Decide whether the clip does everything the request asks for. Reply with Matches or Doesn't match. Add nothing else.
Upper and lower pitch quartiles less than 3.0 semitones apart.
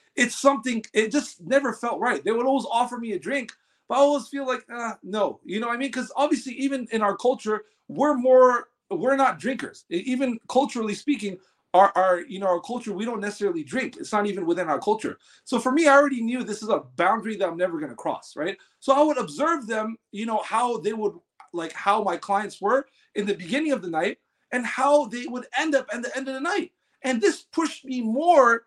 Doesn't match